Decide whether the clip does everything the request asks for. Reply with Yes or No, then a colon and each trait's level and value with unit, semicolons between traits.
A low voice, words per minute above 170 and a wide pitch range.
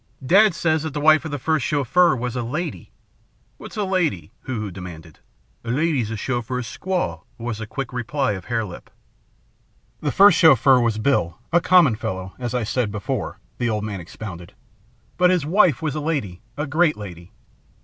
Yes: low, 125 Hz; average, 190 wpm; wide, 6.7 semitones